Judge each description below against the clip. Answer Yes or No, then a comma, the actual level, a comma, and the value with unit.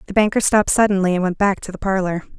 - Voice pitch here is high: Yes, high, 195 Hz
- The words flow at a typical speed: No, fast, 250 wpm